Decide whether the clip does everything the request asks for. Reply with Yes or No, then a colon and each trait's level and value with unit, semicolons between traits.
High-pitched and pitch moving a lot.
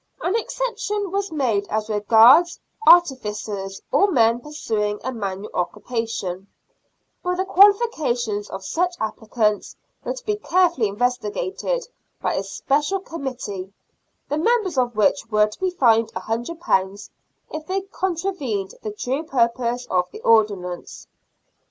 Yes: high, 245 Hz; wide, 9.0 semitones